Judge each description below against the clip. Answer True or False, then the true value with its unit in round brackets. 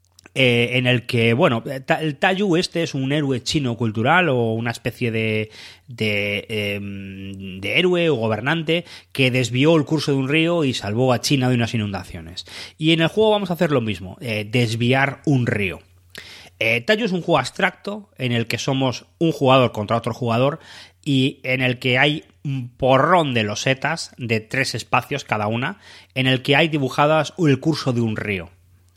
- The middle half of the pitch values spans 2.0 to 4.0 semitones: False (5.3 semitones)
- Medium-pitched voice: False (130 Hz)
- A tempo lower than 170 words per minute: False (185 wpm)